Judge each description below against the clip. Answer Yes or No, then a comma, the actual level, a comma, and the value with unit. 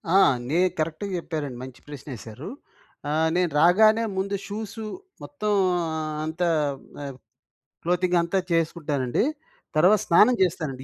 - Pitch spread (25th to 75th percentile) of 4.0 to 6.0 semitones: Yes, average, 4.7 semitones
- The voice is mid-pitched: Yes, medium, 170 Hz